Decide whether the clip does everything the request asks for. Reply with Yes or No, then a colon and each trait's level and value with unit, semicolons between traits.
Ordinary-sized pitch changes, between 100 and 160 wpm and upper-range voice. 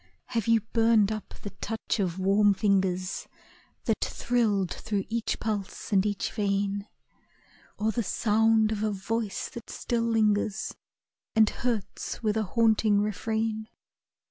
No: narrow, 2.0 semitones; slow, 135 wpm; high, 215 Hz